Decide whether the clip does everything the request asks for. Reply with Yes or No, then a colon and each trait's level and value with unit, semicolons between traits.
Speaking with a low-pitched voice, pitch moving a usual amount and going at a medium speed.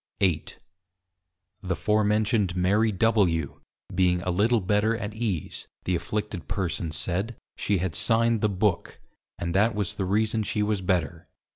Yes: low, 100 Hz; average, 3.2 semitones; average, 150 wpm